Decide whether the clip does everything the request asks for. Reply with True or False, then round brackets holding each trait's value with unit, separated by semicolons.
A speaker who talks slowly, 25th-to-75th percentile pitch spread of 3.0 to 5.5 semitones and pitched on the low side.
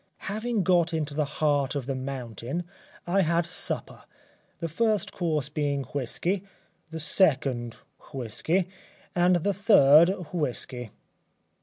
False (120 wpm; 4.6 semitones; 155 Hz)